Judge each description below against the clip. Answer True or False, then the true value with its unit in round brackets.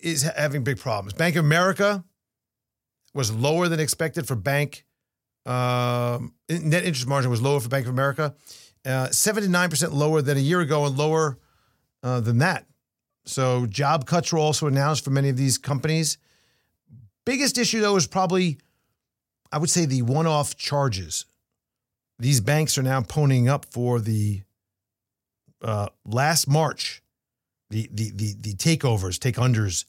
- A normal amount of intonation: True (4.5 semitones)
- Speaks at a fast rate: False (150 wpm)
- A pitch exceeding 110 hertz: True (140 Hz)